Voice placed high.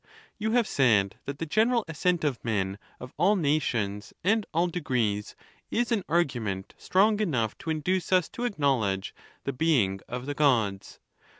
No: medium, 145 Hz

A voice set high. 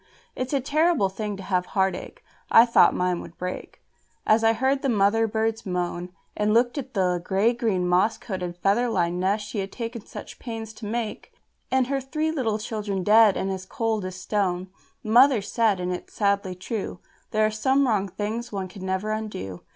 Yes: high, 210 Hz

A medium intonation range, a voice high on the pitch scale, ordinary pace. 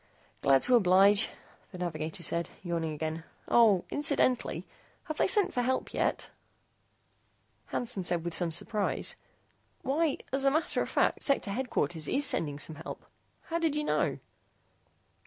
No: wide, 8.5 semitones; high, 200 Hz; average, 145 wpm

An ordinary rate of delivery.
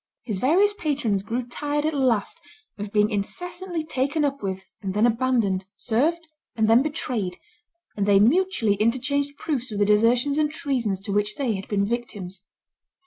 Yes: average, 165 wpm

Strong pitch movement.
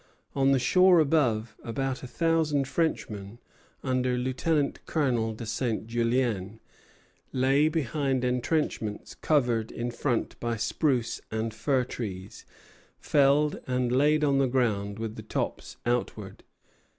No: average, 3.8 semitones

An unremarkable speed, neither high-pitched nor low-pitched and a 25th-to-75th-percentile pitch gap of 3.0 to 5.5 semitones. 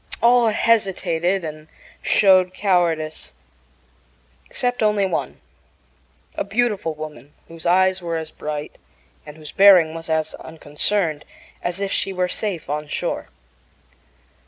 No: slow, 120 wpm; medium, 175 Hz; average, 3.9 semitones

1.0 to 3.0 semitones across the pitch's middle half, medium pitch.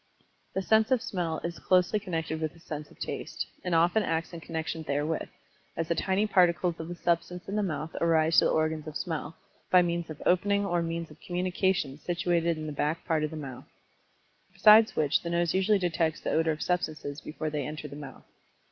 Yes: narrow, 2.4 semitones; medium, 165 Hz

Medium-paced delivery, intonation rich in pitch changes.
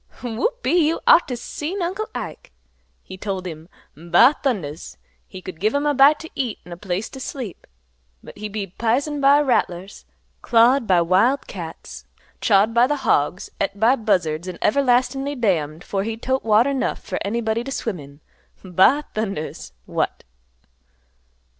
Yes: average, 170 wpm; wide, 6.5 semitones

